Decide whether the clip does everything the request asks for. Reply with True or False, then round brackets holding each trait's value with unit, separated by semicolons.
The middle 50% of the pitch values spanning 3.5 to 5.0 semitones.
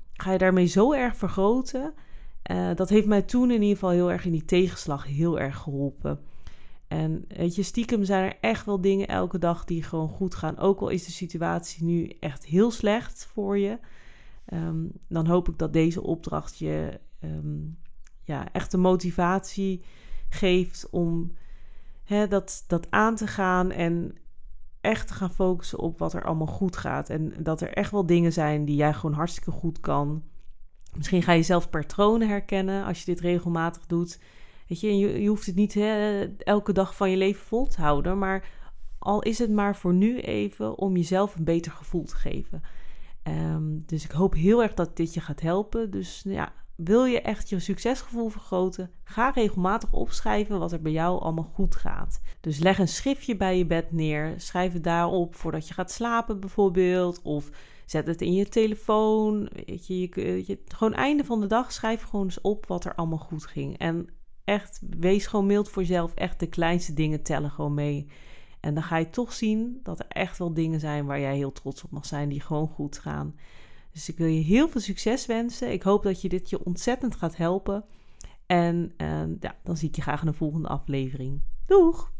True (4.2 semitones)